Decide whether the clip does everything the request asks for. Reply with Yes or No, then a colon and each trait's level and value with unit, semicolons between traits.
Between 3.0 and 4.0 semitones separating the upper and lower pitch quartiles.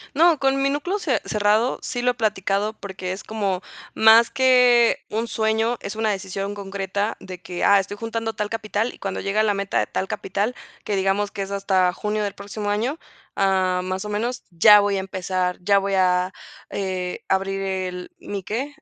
No: narrow, 2.6 semitones